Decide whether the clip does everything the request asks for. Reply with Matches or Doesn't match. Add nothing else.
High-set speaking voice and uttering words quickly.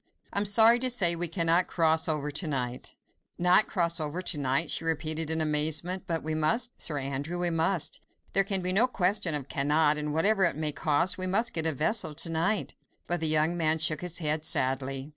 Doesn't match